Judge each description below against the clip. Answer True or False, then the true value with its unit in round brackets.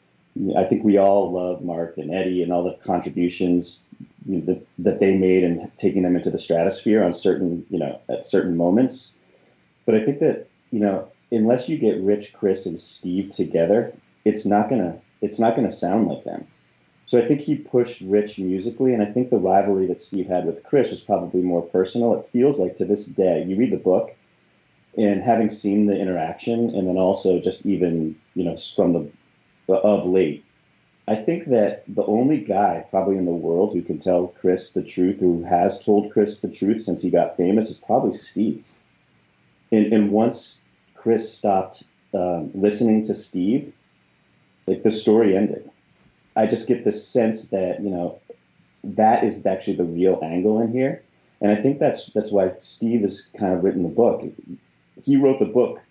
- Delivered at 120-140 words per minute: False (190 wpm)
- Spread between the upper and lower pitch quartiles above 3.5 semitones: False (3.0 semitones)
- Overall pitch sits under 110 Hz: True (95 Hz)